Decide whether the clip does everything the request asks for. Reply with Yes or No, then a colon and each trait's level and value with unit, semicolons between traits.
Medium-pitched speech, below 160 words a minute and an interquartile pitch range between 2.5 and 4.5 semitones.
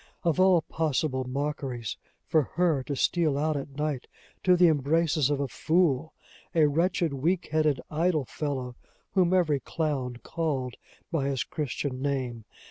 Yes: medium, 150 Hz; average, 145 wpm; average, 3.5 semitones